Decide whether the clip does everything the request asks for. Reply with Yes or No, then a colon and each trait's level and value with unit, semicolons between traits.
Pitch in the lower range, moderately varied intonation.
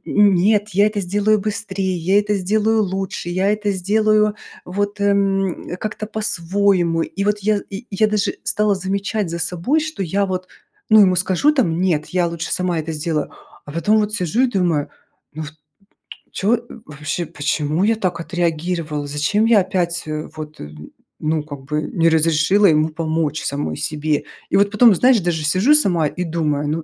No: medium, 185 Hz; average, 4.2 semitones